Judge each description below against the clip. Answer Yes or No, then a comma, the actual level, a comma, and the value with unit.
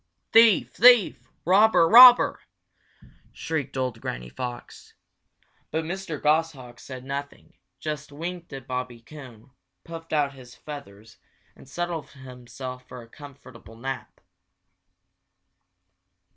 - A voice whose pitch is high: No, medium, 140 Hz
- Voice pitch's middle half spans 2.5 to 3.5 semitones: No, average, 4.5 semitones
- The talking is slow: Yes, slow, 105 wpm